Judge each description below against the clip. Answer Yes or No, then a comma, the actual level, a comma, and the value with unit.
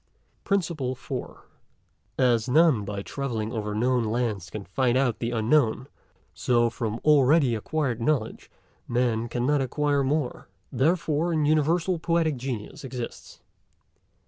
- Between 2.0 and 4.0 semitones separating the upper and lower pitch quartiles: No, average, 4.6 semitones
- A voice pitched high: No, low, 125 Hz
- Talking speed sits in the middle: No, slow, 125 wpm